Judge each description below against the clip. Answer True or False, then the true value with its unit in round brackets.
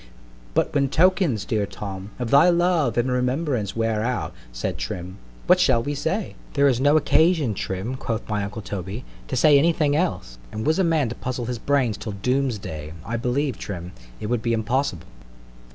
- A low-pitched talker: True (125 Hz)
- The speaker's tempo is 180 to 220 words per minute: True (195 wpm)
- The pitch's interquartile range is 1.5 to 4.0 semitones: False (5.4 semitones)